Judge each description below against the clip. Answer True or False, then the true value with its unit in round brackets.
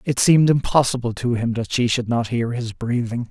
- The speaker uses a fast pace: True (220 wpm)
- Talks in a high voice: False (120 Hz)